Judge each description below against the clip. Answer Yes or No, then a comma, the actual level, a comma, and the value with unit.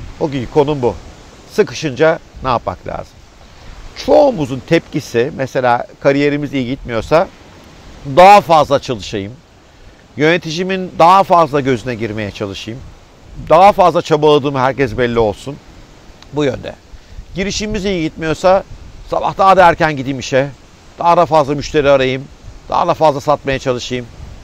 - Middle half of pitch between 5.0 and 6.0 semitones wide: Yes, average, 5.3 semitones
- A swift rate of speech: No, average, 125 wpm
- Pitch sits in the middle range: Yes, medium, 145 Hz